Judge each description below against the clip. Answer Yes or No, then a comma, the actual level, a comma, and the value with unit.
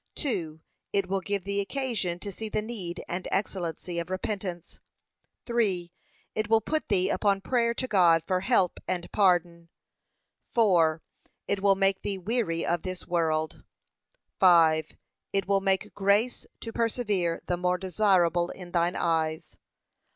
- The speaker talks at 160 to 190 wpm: No, average, 145 wpm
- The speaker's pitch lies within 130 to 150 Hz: No, medium, 185 Hz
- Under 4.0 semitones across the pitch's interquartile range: Yes, average, 2.9 semitones